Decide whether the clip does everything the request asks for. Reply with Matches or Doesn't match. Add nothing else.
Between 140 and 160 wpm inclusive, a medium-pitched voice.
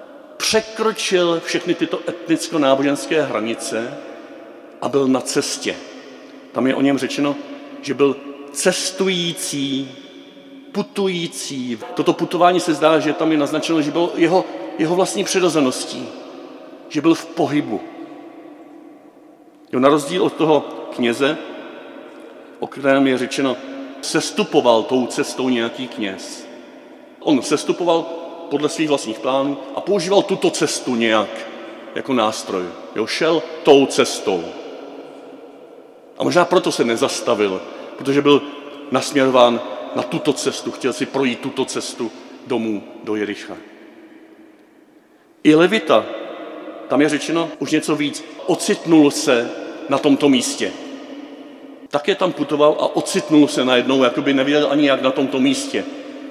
Doesn't match